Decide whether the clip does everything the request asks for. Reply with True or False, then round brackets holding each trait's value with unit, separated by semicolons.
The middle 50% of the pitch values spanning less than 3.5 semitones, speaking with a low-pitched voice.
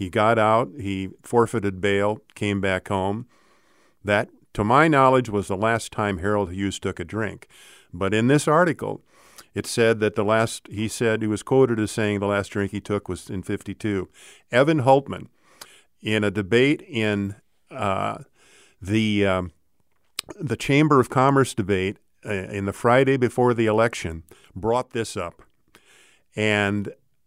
True (2.8 semitones; 105 Hz)